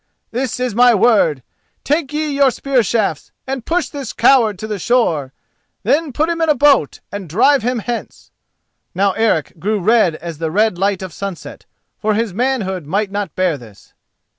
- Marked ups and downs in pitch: Yes, wide, 5.8 semitones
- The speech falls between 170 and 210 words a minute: Yes, average, 180 wpm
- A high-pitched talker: Yes, high, 220 Hz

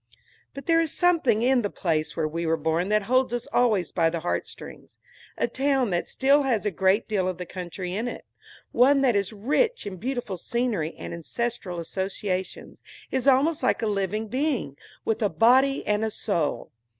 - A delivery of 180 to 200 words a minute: Yes, average, 185 wpm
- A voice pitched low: No, high, 215 Hz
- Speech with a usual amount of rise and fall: No, wide, 6.0 semitones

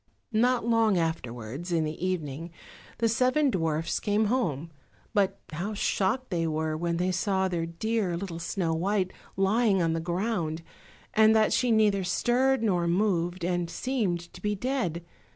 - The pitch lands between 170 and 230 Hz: Yes, medium, 185 Hz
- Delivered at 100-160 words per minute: Yes, average, 155 wpm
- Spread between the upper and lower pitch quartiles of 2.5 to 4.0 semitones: No, average, 4.5 semitones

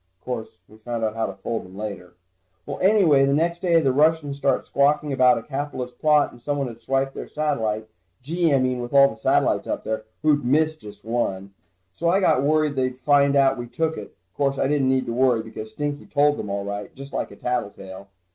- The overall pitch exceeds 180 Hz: No, low, 135 Hz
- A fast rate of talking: Yes, fast, 225 wpm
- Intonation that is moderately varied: Yes, average, 4.6 semitones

